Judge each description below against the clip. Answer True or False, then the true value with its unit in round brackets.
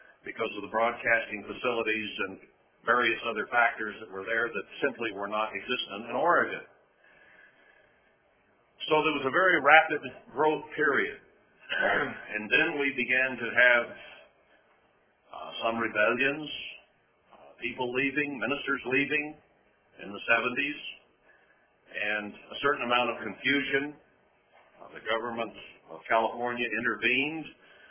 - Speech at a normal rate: False (120 wpm)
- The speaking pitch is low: True (125 Hz)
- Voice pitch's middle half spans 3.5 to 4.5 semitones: True (3.8 semitones)